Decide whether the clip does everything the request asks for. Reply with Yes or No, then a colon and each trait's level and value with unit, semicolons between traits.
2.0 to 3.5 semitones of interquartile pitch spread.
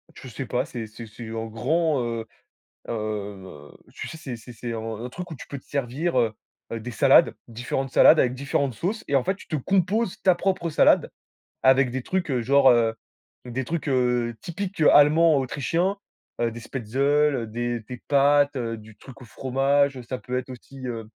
No: average, 3.9 semitones